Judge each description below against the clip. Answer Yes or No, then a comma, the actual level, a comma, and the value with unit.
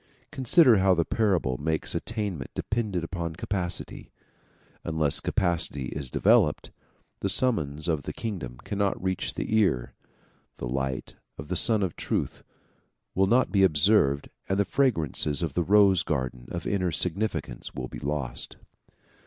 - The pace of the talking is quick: No, average, 145 wpm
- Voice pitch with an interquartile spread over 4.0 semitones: Yes, wide, 5.6 semitones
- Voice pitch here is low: Yes, very low, 90 Hz